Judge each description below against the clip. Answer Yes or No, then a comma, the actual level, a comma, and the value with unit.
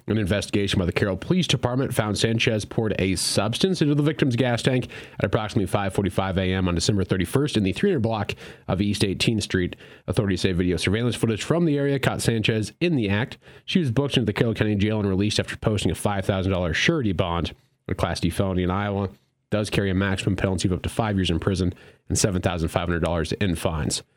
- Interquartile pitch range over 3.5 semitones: Yes, average, 4.3 semitones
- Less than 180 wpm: No, fast, 205 wpm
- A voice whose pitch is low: Yes, low, 105 Hz